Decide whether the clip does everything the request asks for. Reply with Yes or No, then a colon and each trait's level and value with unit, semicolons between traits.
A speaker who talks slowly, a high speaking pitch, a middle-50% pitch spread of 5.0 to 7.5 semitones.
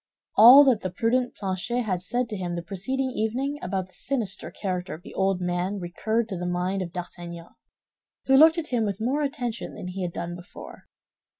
No: average, 200 wpm; high, 195 Hz; wide, 5.5 semitones